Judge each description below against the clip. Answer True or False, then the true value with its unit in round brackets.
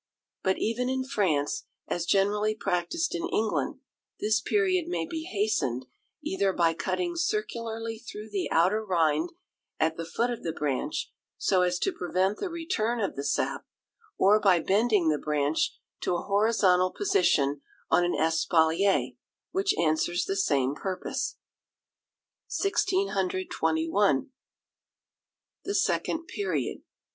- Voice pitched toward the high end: True (200 Hz)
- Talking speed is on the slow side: True (130 wpm)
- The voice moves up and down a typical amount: False (6.6 semitones)